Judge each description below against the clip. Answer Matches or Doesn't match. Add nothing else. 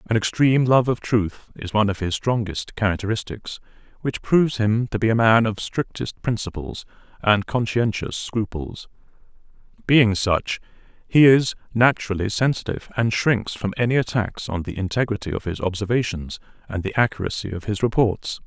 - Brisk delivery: Doesn't match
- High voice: Doesn't match